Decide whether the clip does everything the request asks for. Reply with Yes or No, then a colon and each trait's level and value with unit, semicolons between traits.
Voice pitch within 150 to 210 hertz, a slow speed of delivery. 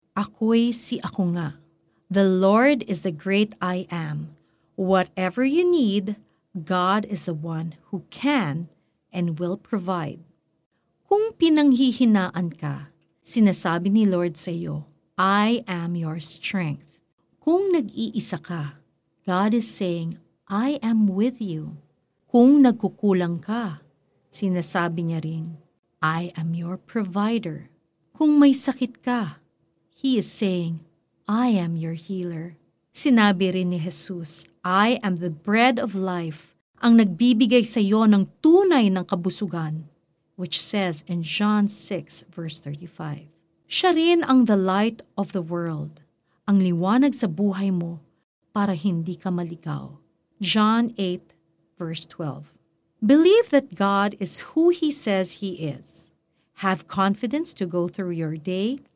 No: medium, 185 Hz; average, 130 wpm